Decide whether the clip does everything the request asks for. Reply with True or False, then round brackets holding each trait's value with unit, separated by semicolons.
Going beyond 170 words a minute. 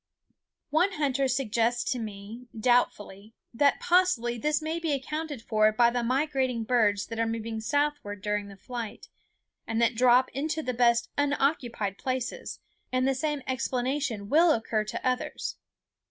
False (150 wpm)